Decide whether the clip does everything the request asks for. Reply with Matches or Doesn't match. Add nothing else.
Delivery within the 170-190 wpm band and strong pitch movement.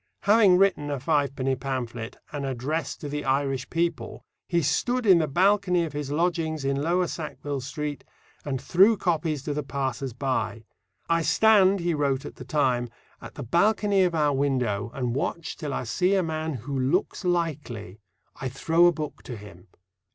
Doesn't match